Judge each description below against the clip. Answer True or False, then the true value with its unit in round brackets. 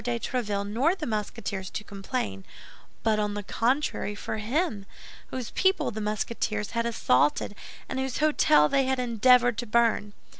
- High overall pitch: True (225 Hz)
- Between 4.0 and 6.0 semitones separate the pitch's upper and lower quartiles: False (3.5 semitones)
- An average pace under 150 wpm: False (155 wpm)